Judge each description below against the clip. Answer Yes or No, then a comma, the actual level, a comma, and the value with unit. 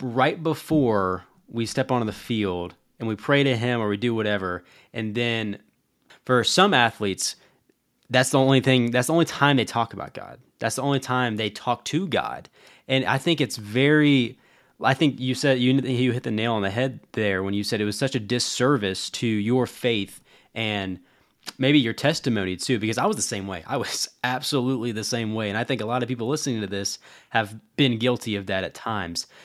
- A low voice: Yes, low, 120 Hz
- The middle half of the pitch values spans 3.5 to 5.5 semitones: Yes, average, 3.8 semitones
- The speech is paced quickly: Yes, fast, 210 wpm